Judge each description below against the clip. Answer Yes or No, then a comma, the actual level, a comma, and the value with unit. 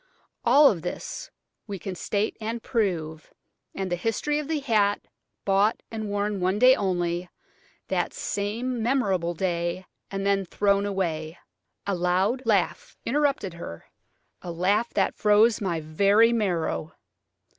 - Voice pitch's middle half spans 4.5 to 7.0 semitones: No, average, 3.9 semitones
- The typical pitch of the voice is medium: No, high, 200 Hz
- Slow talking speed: Yes, slow, 130 wpm